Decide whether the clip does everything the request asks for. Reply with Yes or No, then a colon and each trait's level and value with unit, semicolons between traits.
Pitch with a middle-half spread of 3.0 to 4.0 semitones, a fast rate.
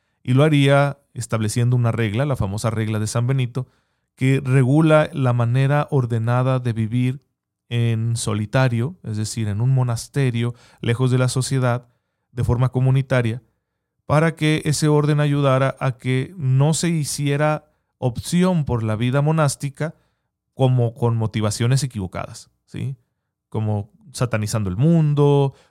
No: average, 3.3 semitones; average, 135 wpm